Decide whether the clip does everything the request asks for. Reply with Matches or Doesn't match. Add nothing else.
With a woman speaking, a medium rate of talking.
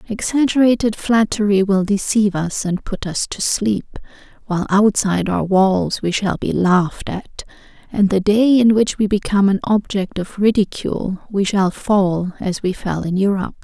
Matches